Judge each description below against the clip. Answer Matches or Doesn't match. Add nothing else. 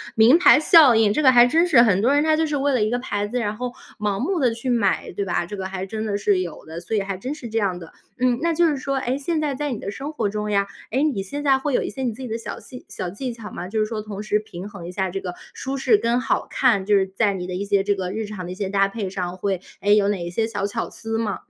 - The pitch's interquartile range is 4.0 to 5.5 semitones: Matches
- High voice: Matches